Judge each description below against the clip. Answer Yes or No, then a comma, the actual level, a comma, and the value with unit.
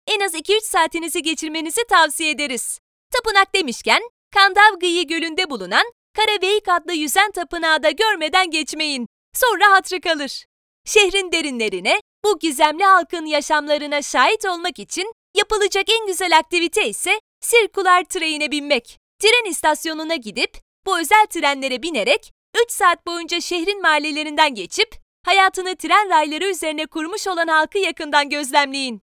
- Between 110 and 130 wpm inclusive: Yes, average, 125 wpm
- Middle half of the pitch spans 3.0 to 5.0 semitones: Yes, average, 4.2 semitones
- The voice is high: Yes, very high, 350 Hz